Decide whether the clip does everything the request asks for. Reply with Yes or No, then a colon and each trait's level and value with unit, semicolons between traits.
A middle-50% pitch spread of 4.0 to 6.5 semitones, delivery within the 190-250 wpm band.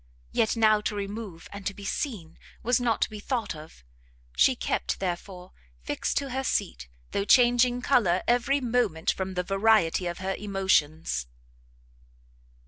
No: average, 4.9 semitones; average, 150 wpm